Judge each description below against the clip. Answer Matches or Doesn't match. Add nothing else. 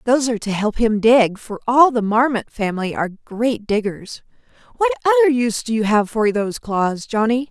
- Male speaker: Doesn't match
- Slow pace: Doesn't match